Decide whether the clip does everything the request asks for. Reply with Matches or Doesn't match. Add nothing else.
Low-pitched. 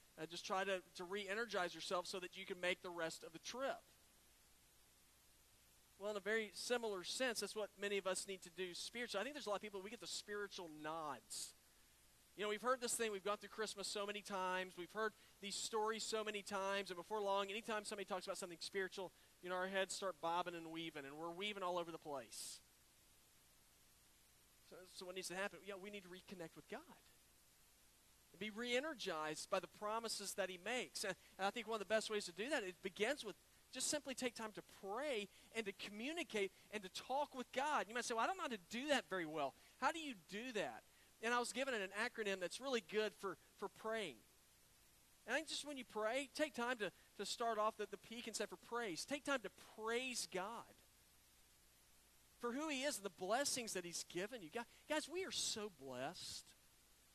Doesn't match